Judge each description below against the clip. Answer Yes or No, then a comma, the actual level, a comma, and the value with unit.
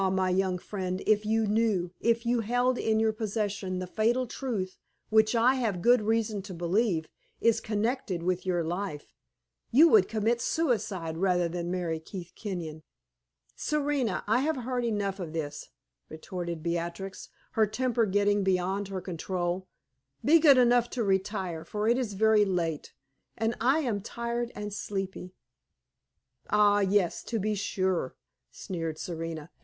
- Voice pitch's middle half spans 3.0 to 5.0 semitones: Yes, average, 4.1 semitones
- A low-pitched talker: No, high, 205 Hz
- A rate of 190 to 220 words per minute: No, average, 150 wpm